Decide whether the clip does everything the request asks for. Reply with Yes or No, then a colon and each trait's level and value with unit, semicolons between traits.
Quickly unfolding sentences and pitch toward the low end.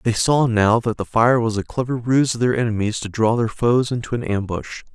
Yes: fast, 245 wpm; low, 115 Hz